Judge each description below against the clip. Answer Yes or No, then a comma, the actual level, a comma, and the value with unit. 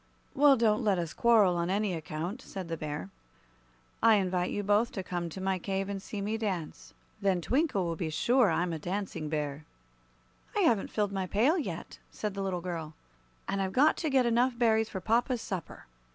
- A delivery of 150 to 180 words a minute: No, average, 195 wpm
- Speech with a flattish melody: No, average, 4.5 semitones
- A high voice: Yes, high, 195 Hz